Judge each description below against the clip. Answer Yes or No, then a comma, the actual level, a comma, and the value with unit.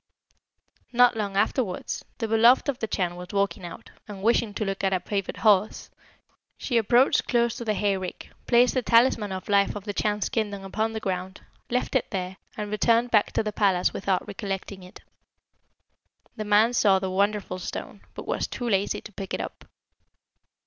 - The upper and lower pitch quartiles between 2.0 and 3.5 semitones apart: Yes, average, 3.0 semitones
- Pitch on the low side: No, high, 205 Hz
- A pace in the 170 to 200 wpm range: Yes, average, 185 wpm